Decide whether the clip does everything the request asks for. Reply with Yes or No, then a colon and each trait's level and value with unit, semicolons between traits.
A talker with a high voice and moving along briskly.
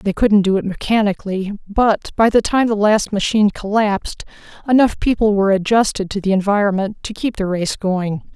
No: high, 205 Hz; average, 180 wpm